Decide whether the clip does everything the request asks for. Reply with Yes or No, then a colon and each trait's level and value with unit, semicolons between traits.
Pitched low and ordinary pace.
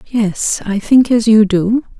No: high, 220 Hz; average, 180 wpm